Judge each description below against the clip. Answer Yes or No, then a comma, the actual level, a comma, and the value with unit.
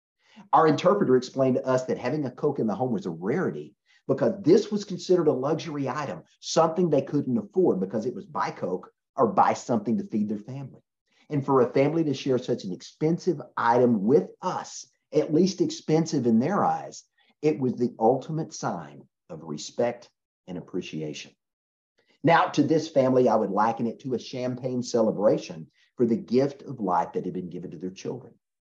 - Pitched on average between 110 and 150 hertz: Yes, low, 135 Hz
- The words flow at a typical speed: Yes, average, 185 wpm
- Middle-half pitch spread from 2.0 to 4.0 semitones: No, average, 4.5 semitones